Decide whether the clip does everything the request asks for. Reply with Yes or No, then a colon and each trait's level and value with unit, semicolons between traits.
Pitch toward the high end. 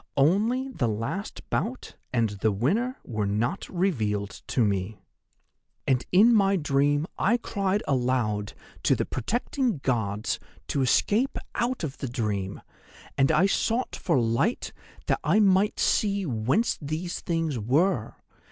No: medium, 145 Hz